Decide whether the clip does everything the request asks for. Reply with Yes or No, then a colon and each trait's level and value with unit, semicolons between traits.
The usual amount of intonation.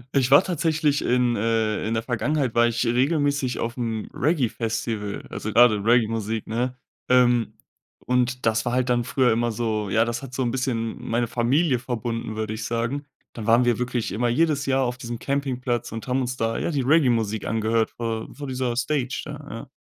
No: narrow, 2.3 semitones